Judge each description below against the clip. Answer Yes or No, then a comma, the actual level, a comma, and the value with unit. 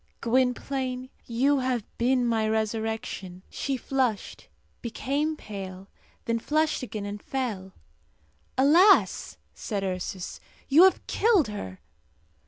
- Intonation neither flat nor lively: Yes, average, 4.5 semitones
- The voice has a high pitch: Yes, high, 240 Hz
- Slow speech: Yes, slow, 105 wpm